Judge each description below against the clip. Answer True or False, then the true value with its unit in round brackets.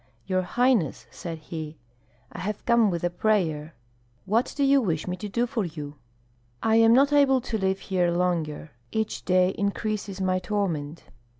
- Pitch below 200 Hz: True (190 Hz)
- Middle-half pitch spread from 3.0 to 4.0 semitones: False (4.6 semitones)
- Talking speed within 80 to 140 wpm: False (170 wpm)